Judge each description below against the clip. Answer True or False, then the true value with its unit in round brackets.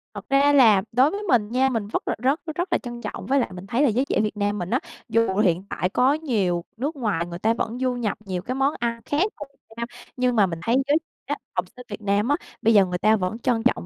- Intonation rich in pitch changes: False (4.5 semitones)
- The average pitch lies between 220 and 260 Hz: True (230 Hz)